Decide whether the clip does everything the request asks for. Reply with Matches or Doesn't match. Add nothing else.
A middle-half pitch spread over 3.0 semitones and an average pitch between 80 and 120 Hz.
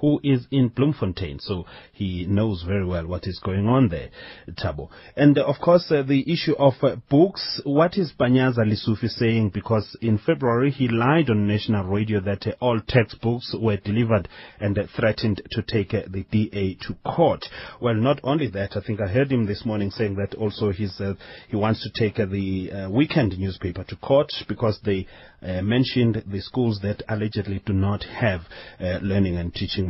Matches